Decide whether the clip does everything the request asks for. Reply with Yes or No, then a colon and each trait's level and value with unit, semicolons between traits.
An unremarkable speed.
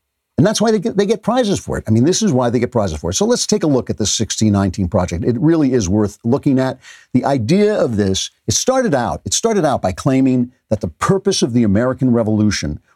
No: fast, 250 wpm